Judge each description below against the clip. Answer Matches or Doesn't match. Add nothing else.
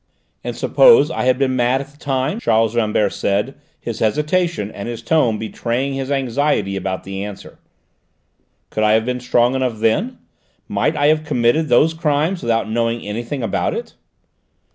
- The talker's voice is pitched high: Doesn't match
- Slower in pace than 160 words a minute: Doesn't match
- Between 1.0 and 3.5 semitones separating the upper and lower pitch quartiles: Doesn't match